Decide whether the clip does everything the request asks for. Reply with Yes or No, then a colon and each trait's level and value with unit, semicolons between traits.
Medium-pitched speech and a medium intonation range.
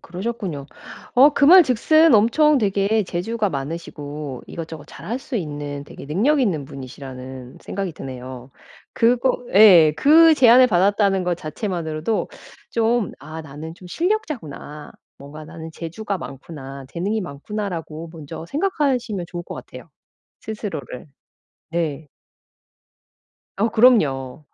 No: medium, 175 Hz; wide, 7.3 semitones